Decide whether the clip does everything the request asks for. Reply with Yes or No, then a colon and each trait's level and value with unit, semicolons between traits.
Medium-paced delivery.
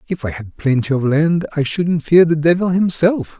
No: fast, 210 wpm